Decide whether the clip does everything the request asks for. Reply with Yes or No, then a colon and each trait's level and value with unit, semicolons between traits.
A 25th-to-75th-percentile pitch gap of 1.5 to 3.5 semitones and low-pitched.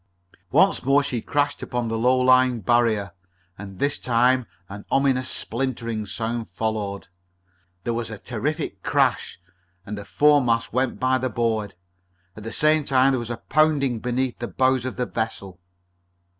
Yes: average, 2.7 semitones; low, 120 Hz